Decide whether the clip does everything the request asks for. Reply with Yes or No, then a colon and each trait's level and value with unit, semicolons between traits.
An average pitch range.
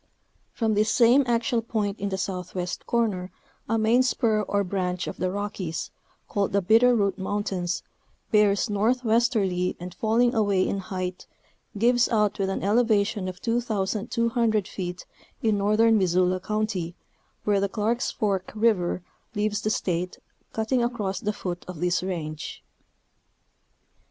Yes: average, 3.4 semitones